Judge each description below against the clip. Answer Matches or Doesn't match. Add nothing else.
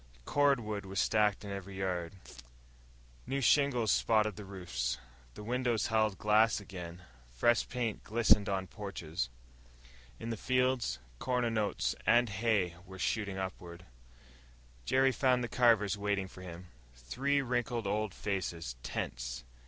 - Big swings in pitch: Doesn't match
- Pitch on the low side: Matches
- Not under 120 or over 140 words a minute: Matches